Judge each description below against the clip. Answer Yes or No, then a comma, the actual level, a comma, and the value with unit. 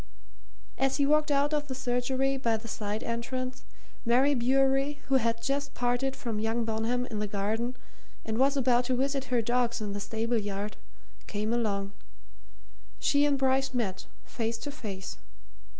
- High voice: Yes, high, 245 Hz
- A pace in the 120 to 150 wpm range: No, average, 165 wpm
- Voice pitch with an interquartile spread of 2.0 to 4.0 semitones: Yes, average, 3.3 semitones